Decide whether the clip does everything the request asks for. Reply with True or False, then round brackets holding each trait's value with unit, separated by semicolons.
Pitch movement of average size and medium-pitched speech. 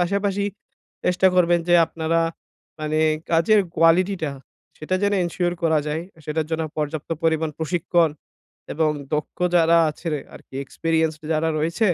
False (1.8 semitones; 165 Hz)